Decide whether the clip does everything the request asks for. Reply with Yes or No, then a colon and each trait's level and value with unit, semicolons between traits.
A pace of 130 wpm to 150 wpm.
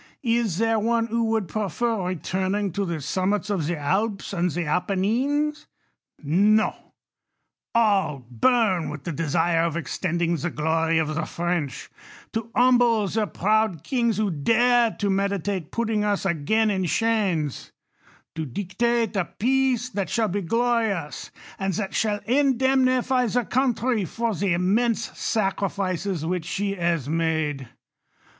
Yes: average, 145 wpm